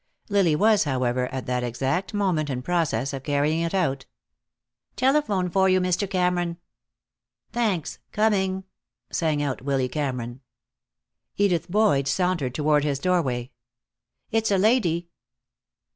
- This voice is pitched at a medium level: Yes, medium, 170 Hz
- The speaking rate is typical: No, slow, 125 wpm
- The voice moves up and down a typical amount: No, wide, 5.8 semitones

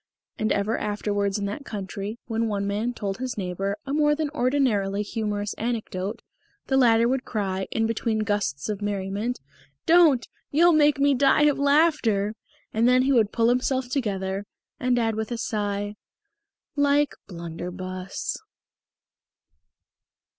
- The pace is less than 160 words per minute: Yes, average, 145 wpm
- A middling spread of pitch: Yes, average, 4.4 semitones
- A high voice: Yes, high, 220 Hz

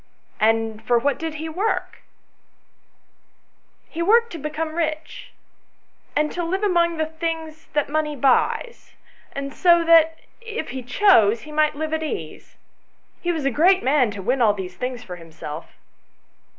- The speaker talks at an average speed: Yes, average, 165 wpm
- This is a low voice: No, very high, 310 Hz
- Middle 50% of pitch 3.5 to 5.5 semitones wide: Yes, average, 5.2 semitones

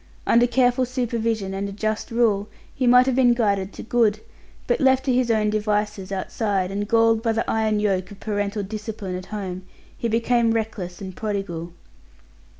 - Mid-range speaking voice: No, high, 215 Hz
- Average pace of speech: Yes, average, 175 wpm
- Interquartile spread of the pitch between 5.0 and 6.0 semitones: No, average, 2.7 semitones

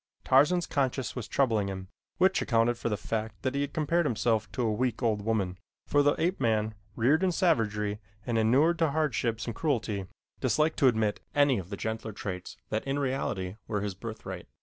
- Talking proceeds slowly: No, average, 190 wpm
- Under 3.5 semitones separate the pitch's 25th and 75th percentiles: No, average, 5.1 semitones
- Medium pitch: No, low, 115 Hz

